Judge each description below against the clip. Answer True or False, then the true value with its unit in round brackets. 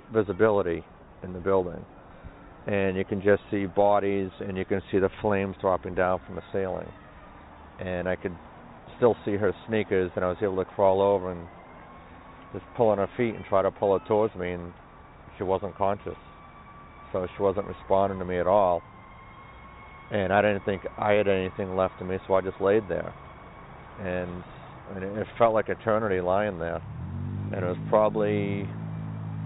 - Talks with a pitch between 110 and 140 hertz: False (95 Hz)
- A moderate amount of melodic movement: False (2.2 semitones)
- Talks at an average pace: True (175 wpm)